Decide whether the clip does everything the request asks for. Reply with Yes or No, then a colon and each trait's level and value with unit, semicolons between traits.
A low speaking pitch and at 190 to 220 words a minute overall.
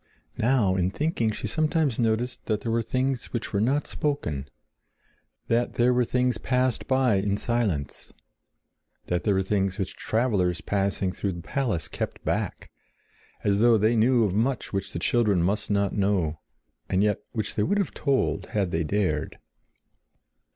No: low, 110 Hz; average, 165 wpm